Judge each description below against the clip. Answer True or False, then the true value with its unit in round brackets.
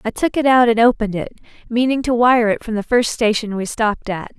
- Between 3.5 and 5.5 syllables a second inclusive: False (5.9 syllables/s)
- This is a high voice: True (230 Hz)